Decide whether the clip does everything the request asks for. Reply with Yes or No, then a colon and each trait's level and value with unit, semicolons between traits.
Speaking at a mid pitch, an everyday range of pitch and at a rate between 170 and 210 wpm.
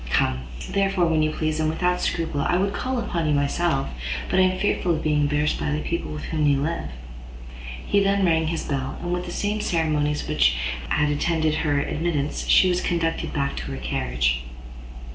Yes: medium, 155 Hz; average, 3.1 semitones; average, 195 wpm